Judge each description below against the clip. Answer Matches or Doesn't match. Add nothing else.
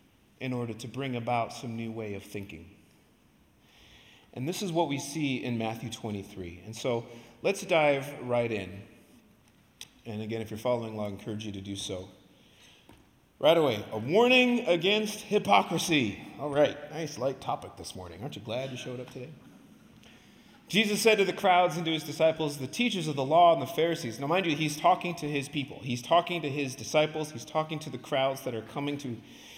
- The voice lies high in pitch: Doesn't match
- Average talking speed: Matches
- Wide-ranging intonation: Matches